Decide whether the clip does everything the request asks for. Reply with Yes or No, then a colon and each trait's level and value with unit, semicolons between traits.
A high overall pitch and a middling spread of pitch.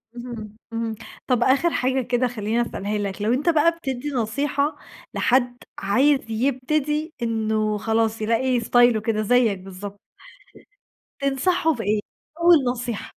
Yes: high, 240 Hz; average, 3.6 semitones